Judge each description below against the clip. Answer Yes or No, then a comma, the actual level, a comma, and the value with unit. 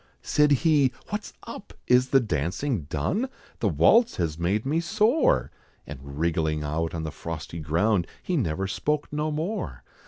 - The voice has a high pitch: No, low, 105 Hz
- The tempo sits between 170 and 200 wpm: No, average, 155 wpm